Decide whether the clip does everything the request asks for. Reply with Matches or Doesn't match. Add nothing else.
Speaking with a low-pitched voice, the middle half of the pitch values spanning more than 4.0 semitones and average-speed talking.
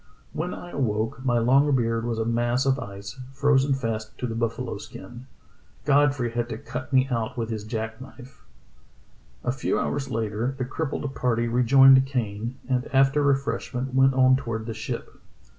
Doesn't match